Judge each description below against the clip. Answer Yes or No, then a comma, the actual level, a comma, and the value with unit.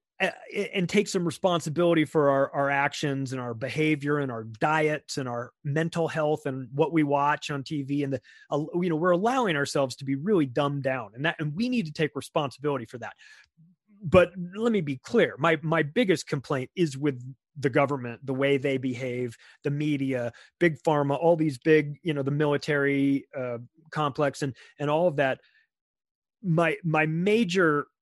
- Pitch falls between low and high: Yes, medium, 150 Hz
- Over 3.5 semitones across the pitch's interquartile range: No, average, 3.0 semitones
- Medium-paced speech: Yes, average, 180 wpm